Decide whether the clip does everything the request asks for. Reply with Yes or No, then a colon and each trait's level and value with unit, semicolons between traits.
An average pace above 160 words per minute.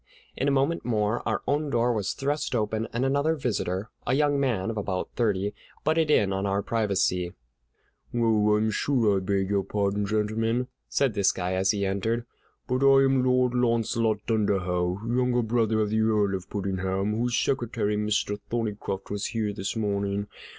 Yes: average, 170 wpm